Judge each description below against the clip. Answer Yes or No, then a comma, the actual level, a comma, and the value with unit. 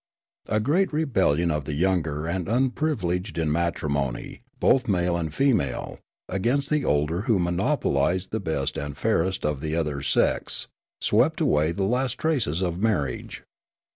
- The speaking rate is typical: Yes, average, 145 wpm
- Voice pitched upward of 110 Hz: No, very low, 90 Hz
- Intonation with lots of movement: Yes, wide, 6.9 semitones